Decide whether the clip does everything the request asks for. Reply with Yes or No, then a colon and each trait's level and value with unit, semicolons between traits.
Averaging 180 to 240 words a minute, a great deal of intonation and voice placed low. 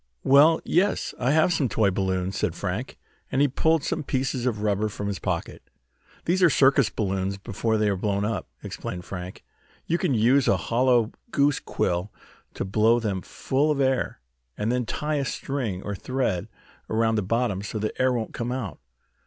No: average, 185 wpm; average, 5.0 semitones; low, 115 Hz